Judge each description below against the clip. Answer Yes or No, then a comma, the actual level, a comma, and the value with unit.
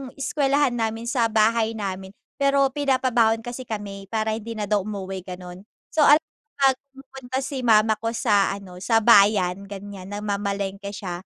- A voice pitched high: Yes, high, 215 Hz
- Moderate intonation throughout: Yes, average, 3.4 semitones